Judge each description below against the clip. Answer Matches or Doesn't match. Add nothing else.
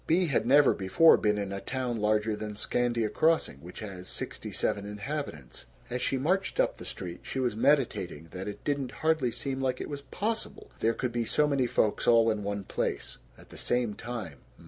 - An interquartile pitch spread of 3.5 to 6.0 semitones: Matches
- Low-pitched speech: Matches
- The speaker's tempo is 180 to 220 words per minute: Matches